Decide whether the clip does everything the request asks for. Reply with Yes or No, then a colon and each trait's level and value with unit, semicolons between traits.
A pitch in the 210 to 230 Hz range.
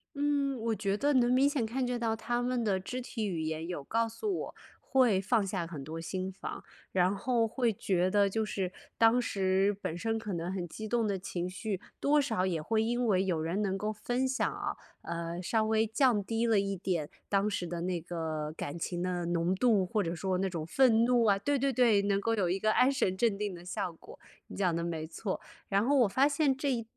No: high, 200 Hz